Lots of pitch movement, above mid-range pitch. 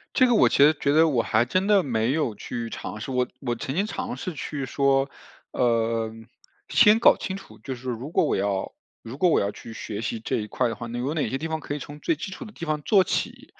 No: wide, 5.9 semitones; low, 135 Hz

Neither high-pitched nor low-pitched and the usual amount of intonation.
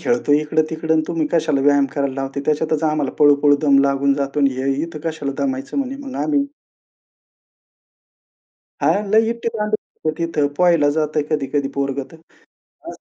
Yes: medium, 150 Hz; average, 3.1 semitones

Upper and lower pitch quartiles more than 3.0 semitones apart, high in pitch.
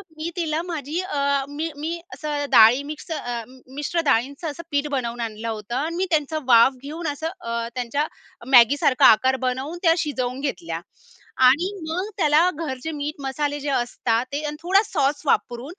Yes: average, 4.2 semitones; very high, 285 Hz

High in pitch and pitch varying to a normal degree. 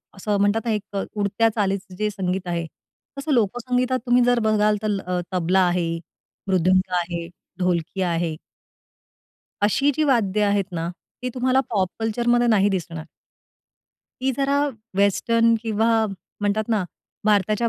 Yes: high, 205 Hz; average, 3.8 semitones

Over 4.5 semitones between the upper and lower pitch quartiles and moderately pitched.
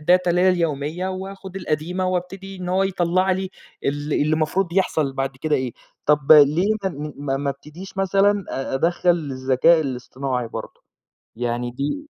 Yes: average, 5.0 semitones; medium, 165 Hz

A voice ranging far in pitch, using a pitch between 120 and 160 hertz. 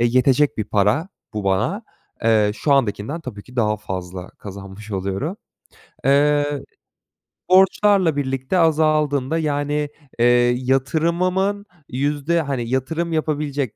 Yes: wide, 5.9 semitones; medium, 140 Hz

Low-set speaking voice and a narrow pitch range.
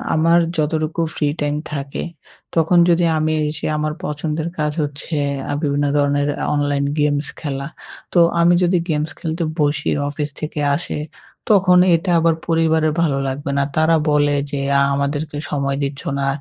No: medium, 150 Hz; narrow, 2.0 semitones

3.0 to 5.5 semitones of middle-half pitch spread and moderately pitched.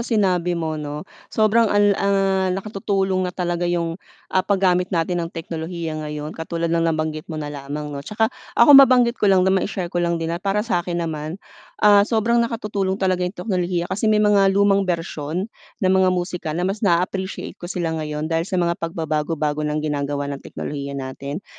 Yes: average, 3.6 semitones; medium, 175 Hz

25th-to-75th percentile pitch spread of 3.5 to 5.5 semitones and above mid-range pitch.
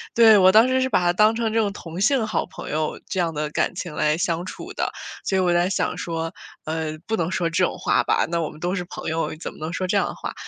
No: average, 4.1 semitones; medium, 180 Hz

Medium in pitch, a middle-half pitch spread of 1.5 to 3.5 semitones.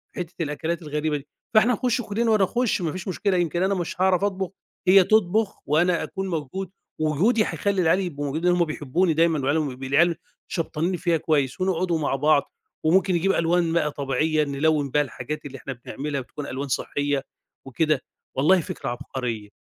No: medium, 165 Hz; average, 4.4 semitones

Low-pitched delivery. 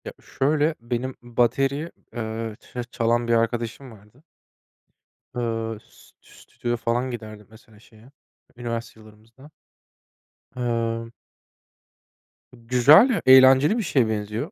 Yes: low, 120 Hz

